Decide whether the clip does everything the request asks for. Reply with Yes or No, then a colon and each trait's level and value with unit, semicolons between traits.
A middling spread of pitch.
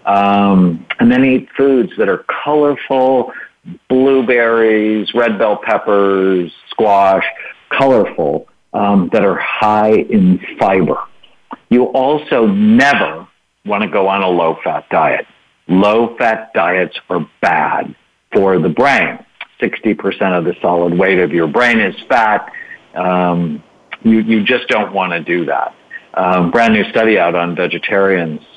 No: wide, 5.9 semitones